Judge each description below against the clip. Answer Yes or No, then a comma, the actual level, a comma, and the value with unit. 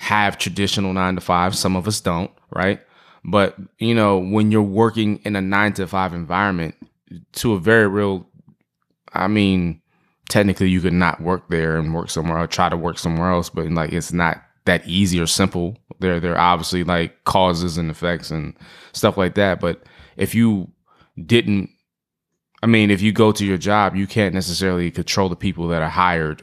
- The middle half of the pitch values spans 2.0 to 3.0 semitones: Yes, average, 2.7 semitones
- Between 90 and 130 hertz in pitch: Yes, very low, 95 Hz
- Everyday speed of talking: Yes, average, 185 wpm